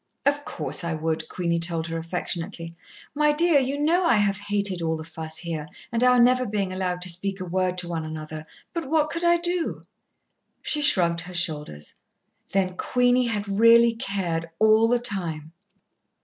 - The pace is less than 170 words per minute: No, average, 175 wpm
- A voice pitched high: Yes, high, 195 Hz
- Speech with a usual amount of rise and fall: No, wide, 6.7 semitones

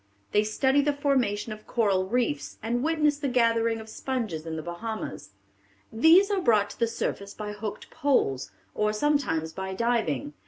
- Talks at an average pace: Yes, average, 165 wpm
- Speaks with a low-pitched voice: No, high, 225 Hz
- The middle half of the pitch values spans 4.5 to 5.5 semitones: Yes, average, 4.9 semitones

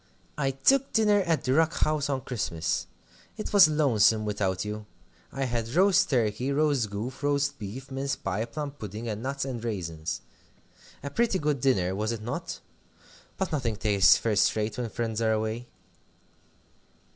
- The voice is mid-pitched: No, low, 120 Hz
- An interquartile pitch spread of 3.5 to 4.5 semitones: No, average, 5.2 semitones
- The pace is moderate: Yes, average, 160 wpm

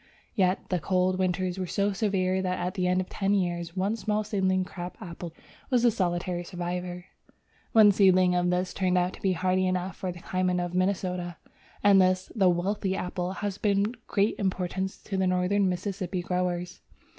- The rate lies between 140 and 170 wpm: No, average, 185 wpm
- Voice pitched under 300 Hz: Yes, medium, 185 Hz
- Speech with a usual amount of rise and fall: No, narrow, 1.5 semitones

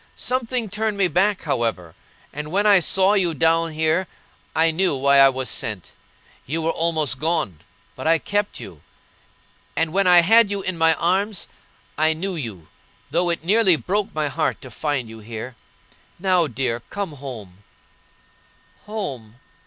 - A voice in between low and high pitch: Yes, medium, 165 Hz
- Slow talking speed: No, average, 160 wpm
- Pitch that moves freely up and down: Yes, wide, 6.0 semitones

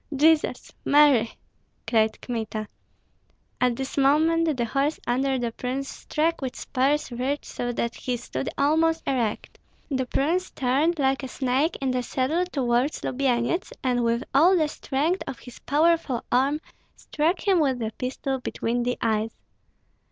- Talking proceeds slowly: No, average, 150 wpm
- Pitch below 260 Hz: No, very high, 265 Hz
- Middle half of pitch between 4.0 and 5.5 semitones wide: No, average, 3.6 semitones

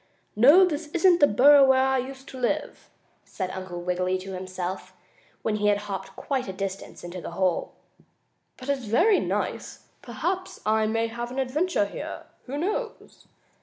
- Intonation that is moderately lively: No, wide, 7.0 semitones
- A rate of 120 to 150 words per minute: No, average, 165 wpm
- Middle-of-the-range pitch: No, high, 240 Hz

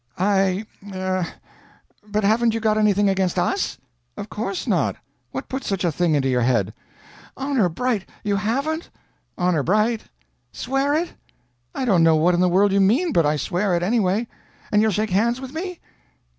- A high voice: Yes, high, 200 Hz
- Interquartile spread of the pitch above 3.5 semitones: Yes, average, 4.6 semitones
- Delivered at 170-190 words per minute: Yes, average, 175 wpm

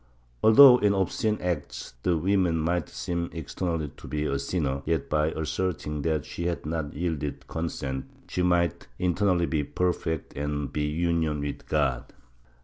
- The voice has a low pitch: Yes, very low, 80 Hz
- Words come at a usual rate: Yes, average, 155 wpm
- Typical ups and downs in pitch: Yes, average, 3.0 semitones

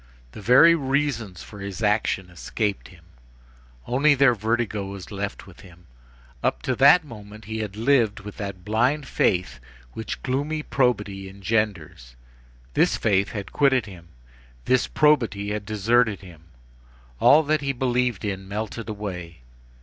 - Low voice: Yes, low, 110 Hz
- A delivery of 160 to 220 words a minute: No, average, 145 wpm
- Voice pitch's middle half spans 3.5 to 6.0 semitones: Yes, average, 4.4 semitones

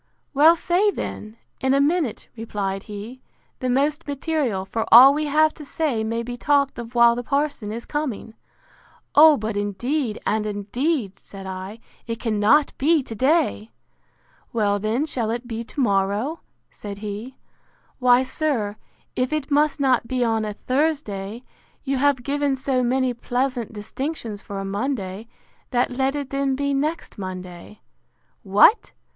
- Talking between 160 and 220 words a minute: No, average, 145 wpm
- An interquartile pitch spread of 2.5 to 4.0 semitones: No, average, 5.0 semitones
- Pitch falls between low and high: No, high, 245 Hz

